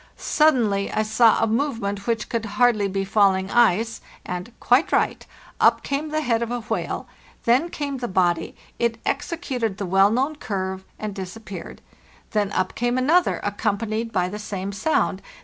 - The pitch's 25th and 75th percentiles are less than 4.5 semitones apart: Yes, average, 3.7 semitones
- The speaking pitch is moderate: No, high, 220 Hz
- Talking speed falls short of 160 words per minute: Yes, average, 150 wpm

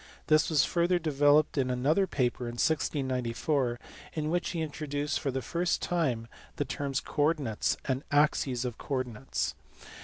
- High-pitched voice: No, medium, 145 Hz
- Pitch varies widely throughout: No, average, 3.4 semitones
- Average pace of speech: Yes, average, 155 wpm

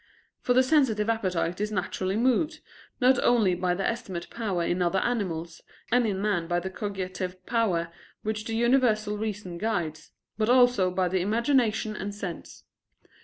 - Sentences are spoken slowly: No, average, 160 wpm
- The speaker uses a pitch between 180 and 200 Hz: No, high, 210 Hz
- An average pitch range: Yes, average, 4.2 semitones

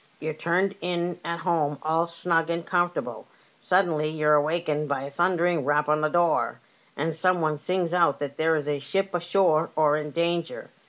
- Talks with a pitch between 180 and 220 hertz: No, medium, 165 Hz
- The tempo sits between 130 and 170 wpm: No, average, 180 wpm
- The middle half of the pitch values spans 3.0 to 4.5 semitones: No, narrow, 2.5 semitones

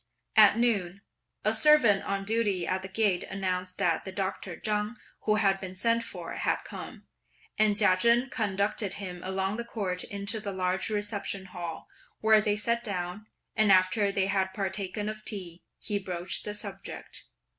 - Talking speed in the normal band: Yes, average, 165 wpm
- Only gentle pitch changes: Yes, narrow, 2.3 semitones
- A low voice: No, high, 200 Hz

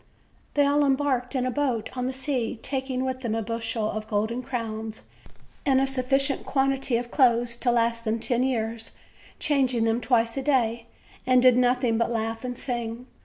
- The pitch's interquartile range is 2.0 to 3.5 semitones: Yes, narrow, 2.5 semitones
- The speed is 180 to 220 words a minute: Yes, average, 185 wpm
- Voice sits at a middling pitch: No, high, 245 Hz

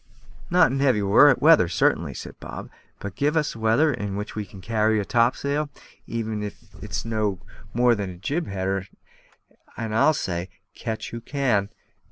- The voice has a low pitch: Yes, low, 110 Hz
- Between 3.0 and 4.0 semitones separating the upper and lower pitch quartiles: No, average, 5.3 semitones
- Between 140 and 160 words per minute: No, average, 170 wpm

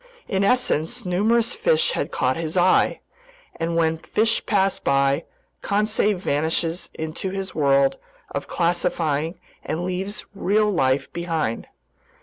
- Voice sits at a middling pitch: Yes, medium, 175 Hz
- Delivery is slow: Yes, slow, 125 wpm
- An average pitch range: Yes, average, 4.1 semitones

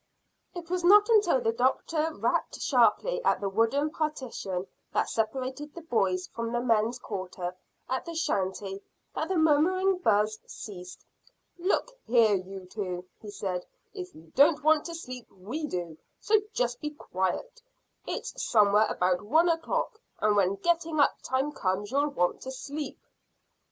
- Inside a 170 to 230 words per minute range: No, average, 155 wpm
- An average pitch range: No, wide, 8.2 semitones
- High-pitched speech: Yes, very high, 250 Hz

